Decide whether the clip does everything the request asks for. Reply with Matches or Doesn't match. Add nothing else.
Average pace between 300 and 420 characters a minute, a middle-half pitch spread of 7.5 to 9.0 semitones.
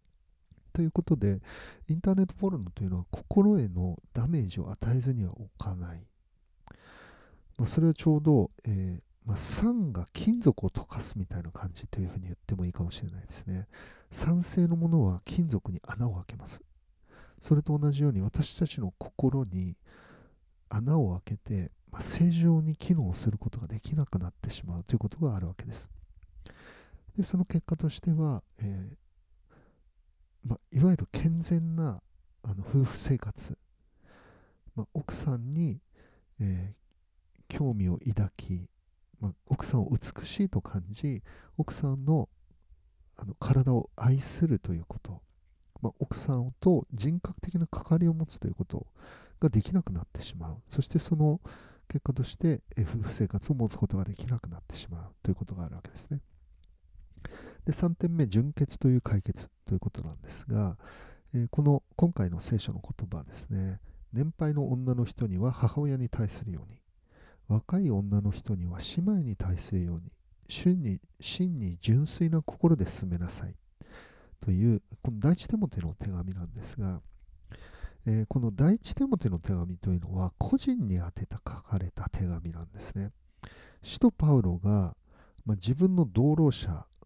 Matches